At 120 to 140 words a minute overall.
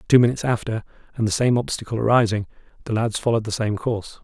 No: average, 200 wpm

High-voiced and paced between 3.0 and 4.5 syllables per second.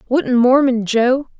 Yes: very high, 250 Hz; 3.6 syllables/s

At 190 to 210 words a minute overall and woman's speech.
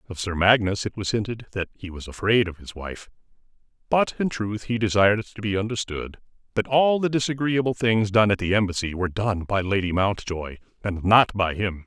No: average, 200 wpm; male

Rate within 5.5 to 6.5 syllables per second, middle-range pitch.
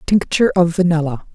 Yes: 5.9 syllables/s; medium, 170 Hz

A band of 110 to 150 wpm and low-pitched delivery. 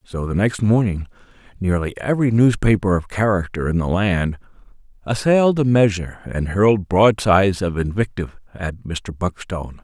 Yes: average, 140 wpm; very low, 95 Hz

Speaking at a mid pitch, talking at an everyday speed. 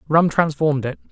Yes: medium, 150 Hz; average, 160 wpm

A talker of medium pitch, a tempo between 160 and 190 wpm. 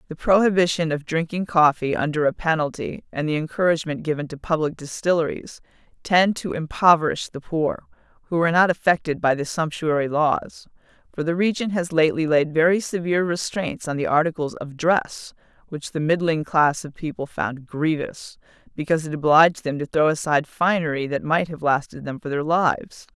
Yes: medium, 160 Hz; average, 170 wpm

